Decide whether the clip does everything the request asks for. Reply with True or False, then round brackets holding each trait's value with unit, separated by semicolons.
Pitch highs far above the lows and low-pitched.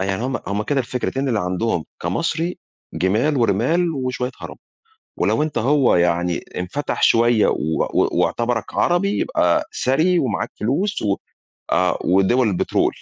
True (7.0 semitones; 120 Hz)